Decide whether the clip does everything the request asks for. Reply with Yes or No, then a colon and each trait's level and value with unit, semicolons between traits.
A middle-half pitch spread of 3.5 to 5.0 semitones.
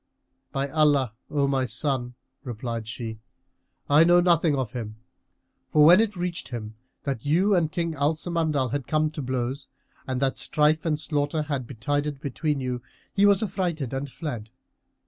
Yes: average, 3.8 semitones